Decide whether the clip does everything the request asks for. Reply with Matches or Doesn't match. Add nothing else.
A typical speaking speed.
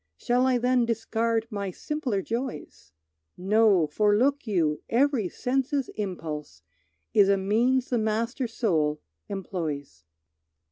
Doesn't match